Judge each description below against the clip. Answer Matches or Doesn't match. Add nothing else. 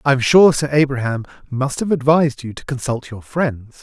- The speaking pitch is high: Doesn't match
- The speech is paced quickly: Doesn't match